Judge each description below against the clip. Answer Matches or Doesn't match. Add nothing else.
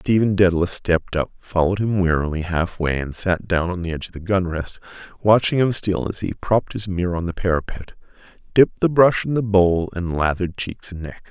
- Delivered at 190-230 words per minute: Matches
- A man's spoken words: Matches